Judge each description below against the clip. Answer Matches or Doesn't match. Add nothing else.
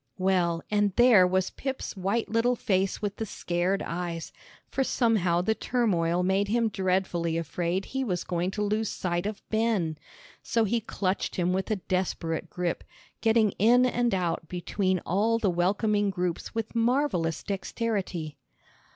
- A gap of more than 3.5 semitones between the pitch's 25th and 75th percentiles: Matches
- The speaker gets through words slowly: Doesn't match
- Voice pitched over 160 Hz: Matches